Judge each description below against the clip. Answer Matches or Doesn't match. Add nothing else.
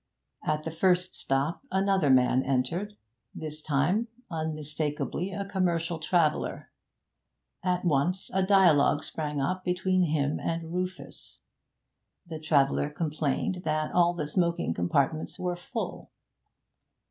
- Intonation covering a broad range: Doesn't match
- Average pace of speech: Doesn't match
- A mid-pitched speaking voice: Matches